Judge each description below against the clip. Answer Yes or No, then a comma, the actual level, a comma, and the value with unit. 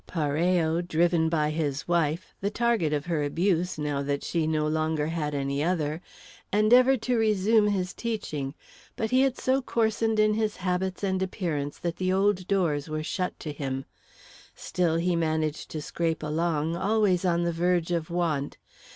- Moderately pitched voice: Yes, medium, 170 Hz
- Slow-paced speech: No, average, 165 wpm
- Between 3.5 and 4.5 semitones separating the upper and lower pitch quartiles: Yes, average, 4.0 semitones